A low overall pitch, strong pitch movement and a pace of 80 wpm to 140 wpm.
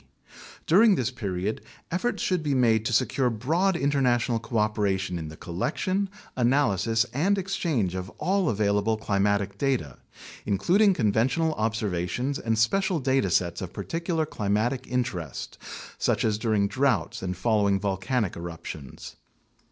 Yes: low, 115 Hz; wide, 6.1 semitones; slow, 135 wpm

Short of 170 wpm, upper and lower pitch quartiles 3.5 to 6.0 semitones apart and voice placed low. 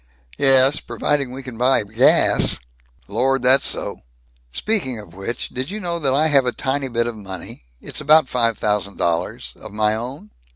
No: average, 190 wpm; average, 4.3 semitones; low, 125 Hz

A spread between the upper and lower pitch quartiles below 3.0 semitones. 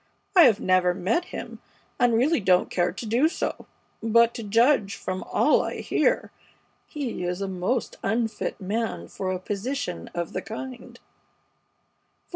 No: average, 4.6 semitones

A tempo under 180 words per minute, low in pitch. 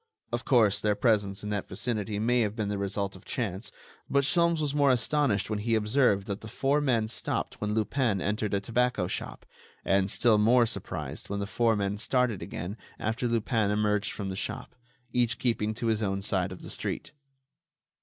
No: average, 195 wpm; low, 110 Hz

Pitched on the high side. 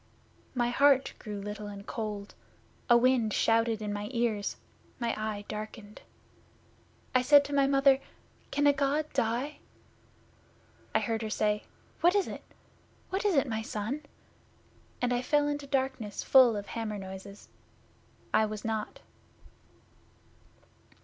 Yes: high, 230 Hz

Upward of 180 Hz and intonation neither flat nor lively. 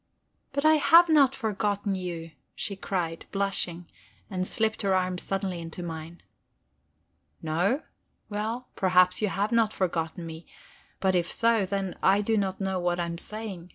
Yes: high, 190 Hz; average, 3.3 semitones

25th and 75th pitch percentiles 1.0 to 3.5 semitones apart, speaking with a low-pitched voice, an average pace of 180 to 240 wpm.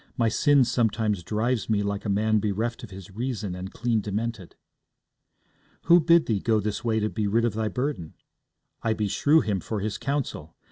Yes: average, 2.7 semitones; low, 110 Hz; average, 185 wpm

